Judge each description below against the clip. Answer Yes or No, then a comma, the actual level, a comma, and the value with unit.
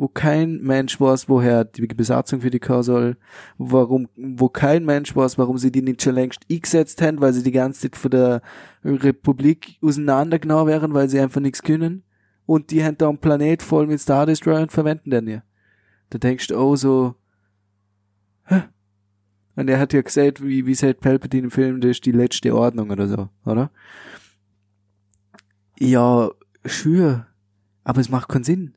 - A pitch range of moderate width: Yes, average, 3.9 semitones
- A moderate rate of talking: Yes, average, 175 wpm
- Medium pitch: No, low, 130 Hz